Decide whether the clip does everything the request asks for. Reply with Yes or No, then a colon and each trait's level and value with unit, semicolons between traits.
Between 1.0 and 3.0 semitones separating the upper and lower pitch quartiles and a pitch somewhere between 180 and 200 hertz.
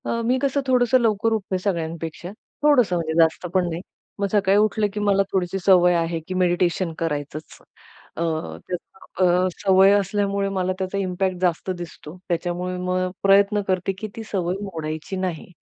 Yes: narrow, 2.6 semitones; medium, 185 Hz